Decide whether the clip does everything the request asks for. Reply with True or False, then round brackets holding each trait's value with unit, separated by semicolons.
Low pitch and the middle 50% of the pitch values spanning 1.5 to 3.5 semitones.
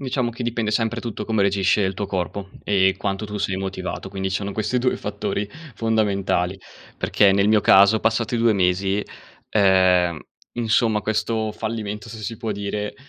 True (105 Hz; 2.5 semitones)